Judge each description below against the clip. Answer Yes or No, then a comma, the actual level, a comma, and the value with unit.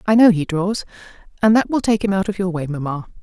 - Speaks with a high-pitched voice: Yes, high, 195 Hz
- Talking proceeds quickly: Yes, fast, 260 wpm